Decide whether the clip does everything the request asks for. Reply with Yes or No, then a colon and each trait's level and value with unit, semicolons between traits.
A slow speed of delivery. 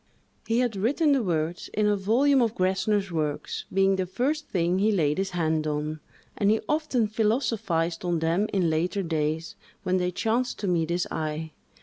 No: average, 185 wpm